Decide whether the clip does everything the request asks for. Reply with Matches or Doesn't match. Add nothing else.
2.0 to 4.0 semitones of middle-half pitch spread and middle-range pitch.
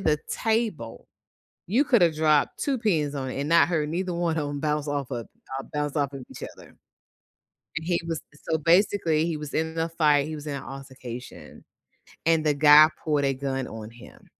Matches